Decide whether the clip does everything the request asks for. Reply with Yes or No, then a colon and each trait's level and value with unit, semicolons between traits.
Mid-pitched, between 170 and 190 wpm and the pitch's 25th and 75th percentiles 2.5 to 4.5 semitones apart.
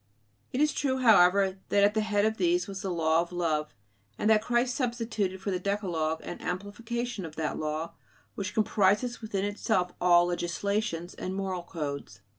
No: high, 195 Hz; average, 175 wpm; average, 4.0 semitones